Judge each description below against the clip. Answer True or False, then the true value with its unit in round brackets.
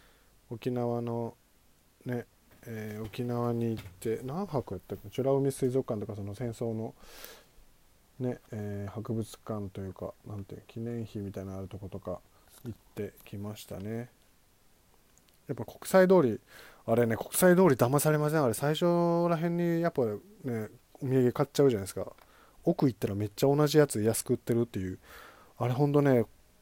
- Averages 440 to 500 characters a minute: False (315 characters per minute)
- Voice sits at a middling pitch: False (120 Hz)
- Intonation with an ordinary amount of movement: True (4.7 semitones)